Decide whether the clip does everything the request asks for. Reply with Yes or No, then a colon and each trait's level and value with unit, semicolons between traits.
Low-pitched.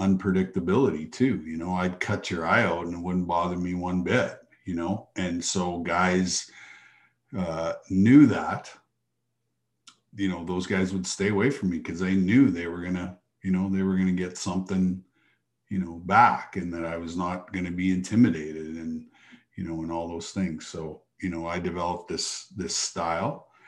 Yes: very low, 90 Hz